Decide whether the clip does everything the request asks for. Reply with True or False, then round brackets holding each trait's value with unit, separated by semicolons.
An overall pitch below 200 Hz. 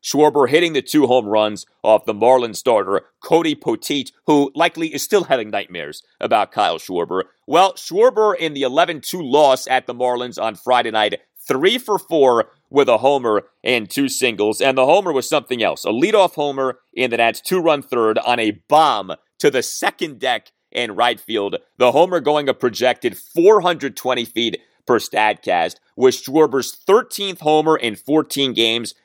True (135 Hz)